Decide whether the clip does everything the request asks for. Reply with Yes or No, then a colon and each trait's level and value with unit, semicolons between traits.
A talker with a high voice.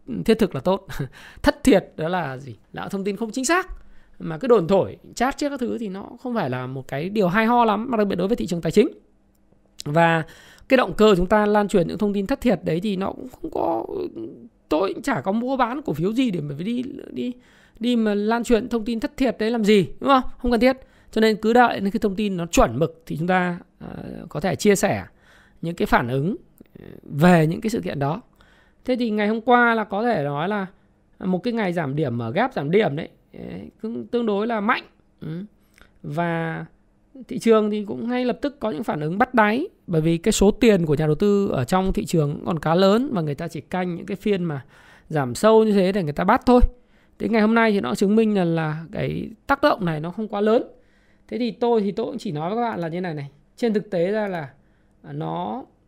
Yes: high, 210 Hz